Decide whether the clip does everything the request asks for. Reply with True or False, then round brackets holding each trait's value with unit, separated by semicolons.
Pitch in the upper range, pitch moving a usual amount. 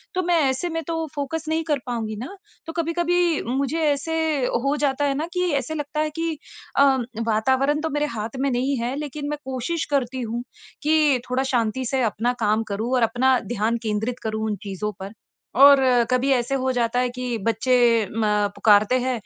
True (265 Hz; 4.2 semitones)